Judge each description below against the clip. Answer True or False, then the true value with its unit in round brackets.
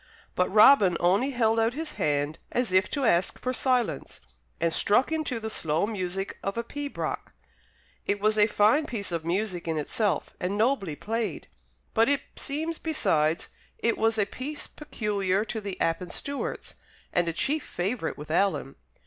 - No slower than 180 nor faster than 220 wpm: False (165 wpm)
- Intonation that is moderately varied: False (5.7 semitones)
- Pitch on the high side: True (210 Hz)